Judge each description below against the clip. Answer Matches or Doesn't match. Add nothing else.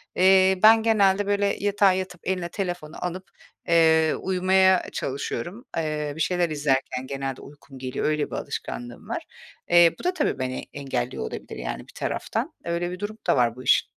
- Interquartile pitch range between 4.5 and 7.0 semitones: Matches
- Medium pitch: Matches